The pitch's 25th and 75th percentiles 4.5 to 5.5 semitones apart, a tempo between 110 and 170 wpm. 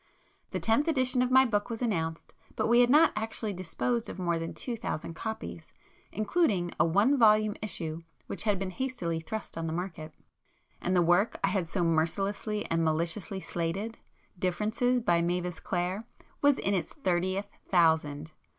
Yes: average, 4.9 semitones; average, 165 wpm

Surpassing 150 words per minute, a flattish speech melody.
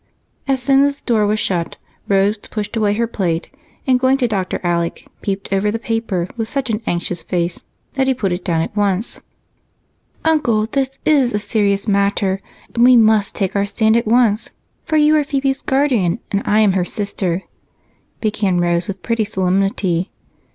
No: average, 185 wpm; average, 4.0 semitones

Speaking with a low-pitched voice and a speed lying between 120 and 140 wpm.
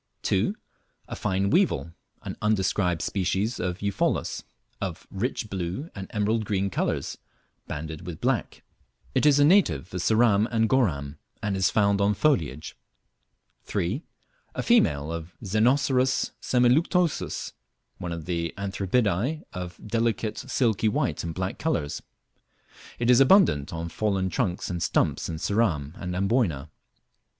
Yes: low, 100 Hz; slow, 135 wpm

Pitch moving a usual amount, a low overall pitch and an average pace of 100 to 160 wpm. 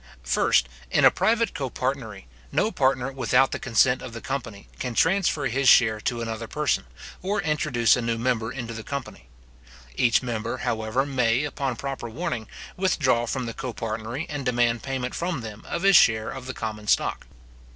No: average, 3.3 semitones; low, 125 Hz; average, 170 wpm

